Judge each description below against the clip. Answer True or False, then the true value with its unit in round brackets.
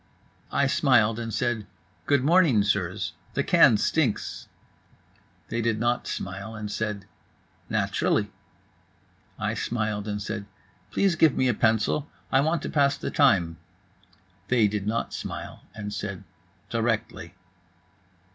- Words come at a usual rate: False (130 wpm)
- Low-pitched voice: True (110 Hz)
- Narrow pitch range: False (4.2 semitones)